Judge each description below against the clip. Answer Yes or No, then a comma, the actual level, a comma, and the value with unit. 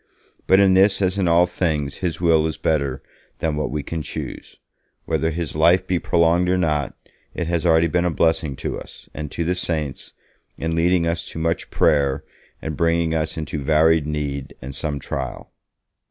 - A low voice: Yes, very low, 80 Hz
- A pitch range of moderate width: No, narrow, 2.2 semitones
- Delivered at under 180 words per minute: No, average, 185 wpm